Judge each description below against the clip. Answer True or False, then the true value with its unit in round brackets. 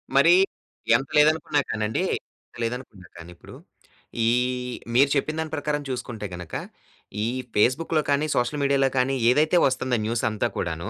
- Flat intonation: False (4.3 semitones)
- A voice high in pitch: False (125 Hz)